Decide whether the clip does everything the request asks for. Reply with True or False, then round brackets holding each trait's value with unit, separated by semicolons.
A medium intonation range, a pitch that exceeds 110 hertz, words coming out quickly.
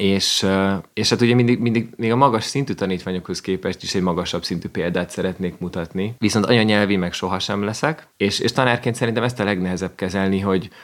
False (3.8 semitones; 100 Hz; 185 wpm)